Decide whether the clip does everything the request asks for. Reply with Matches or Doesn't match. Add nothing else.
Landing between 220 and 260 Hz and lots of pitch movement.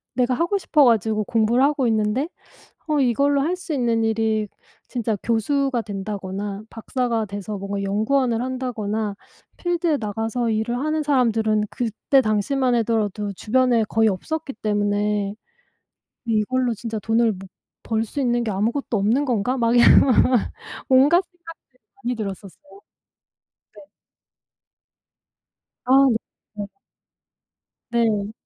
Doesn't match